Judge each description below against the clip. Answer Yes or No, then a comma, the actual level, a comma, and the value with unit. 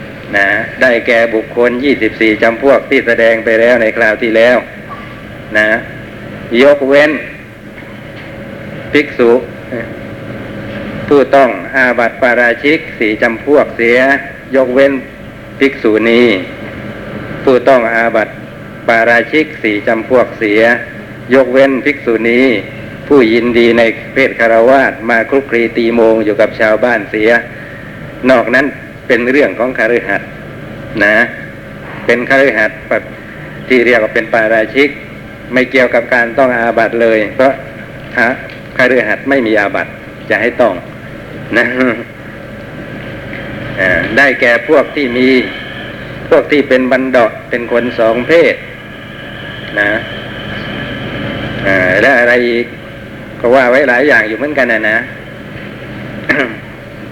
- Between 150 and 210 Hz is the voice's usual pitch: No, low, 120 Hz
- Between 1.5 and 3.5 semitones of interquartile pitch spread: Yes, average, 3.0 semitones